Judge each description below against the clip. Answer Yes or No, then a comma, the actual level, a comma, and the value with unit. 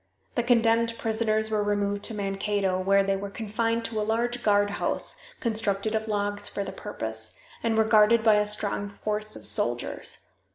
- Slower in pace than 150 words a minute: No, average, 170 wpm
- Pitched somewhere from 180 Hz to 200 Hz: No, high, 210 Hz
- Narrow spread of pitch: Yes, narrow, 1.7 semitones